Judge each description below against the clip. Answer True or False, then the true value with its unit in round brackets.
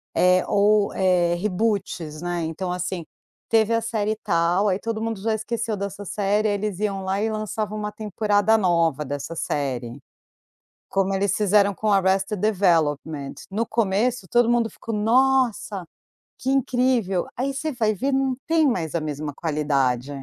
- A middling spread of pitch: True (4.1 semitones)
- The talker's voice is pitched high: True (200 Hz)